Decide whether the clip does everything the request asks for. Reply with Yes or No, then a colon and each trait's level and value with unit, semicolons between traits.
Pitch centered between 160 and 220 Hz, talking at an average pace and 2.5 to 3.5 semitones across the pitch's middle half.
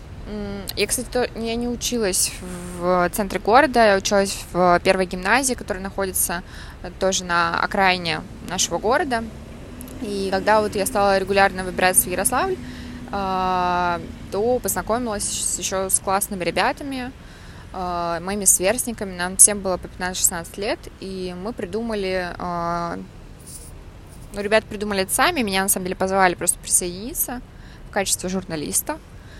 Yes: high, 190 Hz; average, 120 wpm; average, 2.8 semitones